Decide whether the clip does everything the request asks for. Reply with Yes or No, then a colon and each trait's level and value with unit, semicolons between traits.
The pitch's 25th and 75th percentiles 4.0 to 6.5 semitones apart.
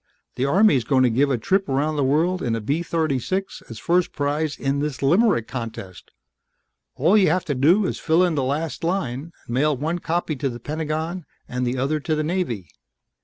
Yes: average, 4.4 semitones